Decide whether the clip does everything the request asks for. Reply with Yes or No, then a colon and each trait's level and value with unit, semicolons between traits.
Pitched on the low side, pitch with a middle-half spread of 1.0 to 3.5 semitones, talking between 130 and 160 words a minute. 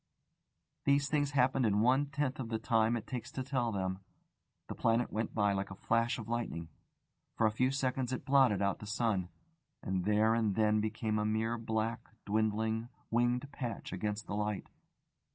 No: low, 110 Hz; average, 2.8 semitones; average, 180 wpm